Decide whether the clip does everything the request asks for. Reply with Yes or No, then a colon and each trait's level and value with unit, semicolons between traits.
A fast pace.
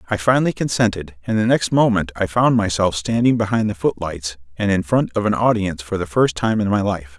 Yes: fast, 225 wpm